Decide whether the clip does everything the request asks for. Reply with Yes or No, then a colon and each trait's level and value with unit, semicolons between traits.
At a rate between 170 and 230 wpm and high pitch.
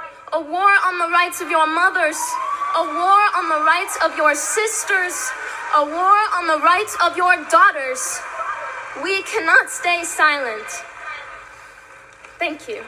No: average, 140 wpm; very high, 345 Hz